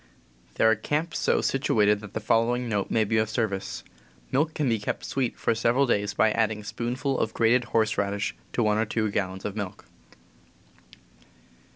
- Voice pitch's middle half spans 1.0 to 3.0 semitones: Yes, narrow, 2.6 semitones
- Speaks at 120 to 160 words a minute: No, average, 190 wpm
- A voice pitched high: No, low, 110 Hz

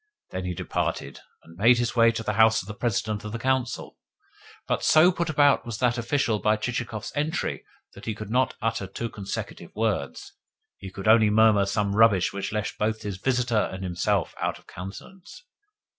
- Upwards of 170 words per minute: Yes, average, 190 wpm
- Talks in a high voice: No, low, 110 Hz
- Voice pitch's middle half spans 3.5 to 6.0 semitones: No, average, 3.0 semitones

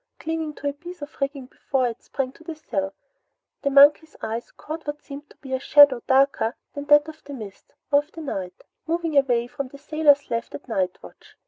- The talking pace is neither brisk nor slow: No, fast, 215 wpm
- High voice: Yes, very high, 280 Hz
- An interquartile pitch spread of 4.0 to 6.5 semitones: No, average, 3.1 semitones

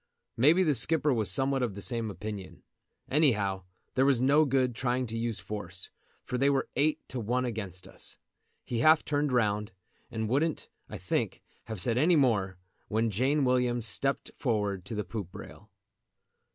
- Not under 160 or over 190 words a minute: Yes, average, 170 wpm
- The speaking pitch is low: Yes, low, 120 Hz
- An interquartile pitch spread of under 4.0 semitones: No, average, 4.4 semitones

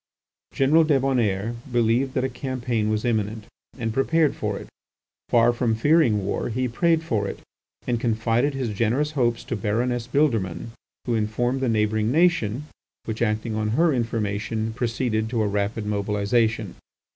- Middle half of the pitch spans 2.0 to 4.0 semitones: Yes, average, 3.2 semitones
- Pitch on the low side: Yes, low, 115 Hz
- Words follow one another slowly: No, average, 150 wpm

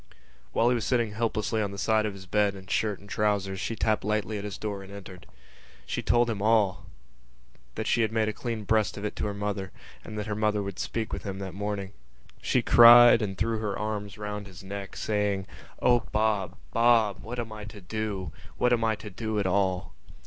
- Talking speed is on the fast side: Yes, fast, 220 wpm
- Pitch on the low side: Yes, low, 105 Hz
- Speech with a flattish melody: Yes, narrow, 1.9 semitones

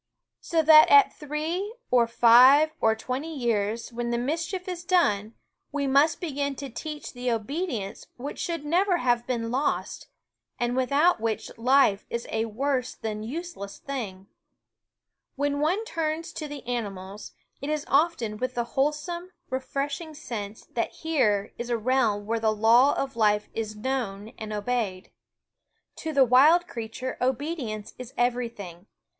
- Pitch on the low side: No, very high, 255 Hz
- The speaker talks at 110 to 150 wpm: No, average, 160 wpm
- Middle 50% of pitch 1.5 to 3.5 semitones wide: No, average, 5.1 semitones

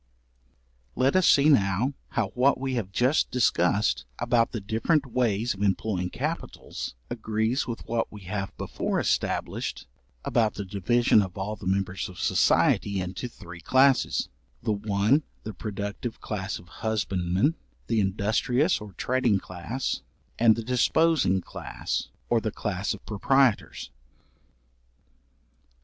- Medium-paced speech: No, slow, 130 wpm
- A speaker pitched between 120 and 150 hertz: No, low, 110 Hz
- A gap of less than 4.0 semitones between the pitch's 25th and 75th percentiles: No, average, 4.3 semitones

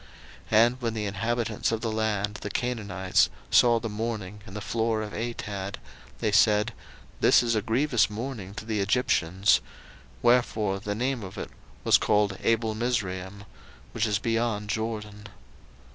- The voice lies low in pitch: Yes, low, 110 Hz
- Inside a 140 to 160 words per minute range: Yes, average, 150 wpm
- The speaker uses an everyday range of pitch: No, narrow, 2.1 semitones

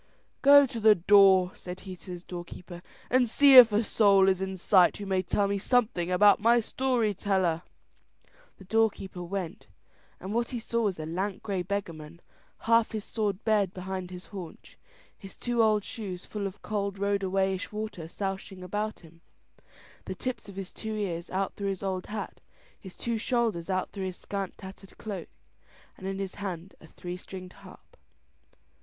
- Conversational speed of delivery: Yes, average, 180 wpm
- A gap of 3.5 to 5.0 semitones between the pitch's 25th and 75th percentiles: No, average, 2.7 semitones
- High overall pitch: Yes, high, 195 Hz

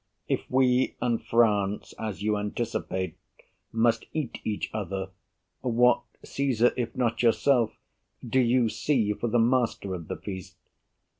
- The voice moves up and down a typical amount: Yes, average, 3.0 semitones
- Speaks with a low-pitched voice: Yes, low, 115 Hz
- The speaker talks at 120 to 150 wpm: Yes, slow, 135 wpm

